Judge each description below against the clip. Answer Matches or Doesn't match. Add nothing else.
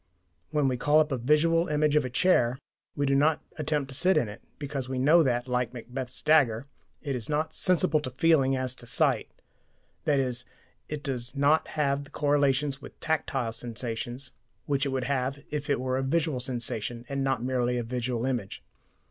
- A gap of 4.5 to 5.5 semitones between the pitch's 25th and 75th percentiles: Doesn't match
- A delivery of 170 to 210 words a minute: Matches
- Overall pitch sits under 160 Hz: Matches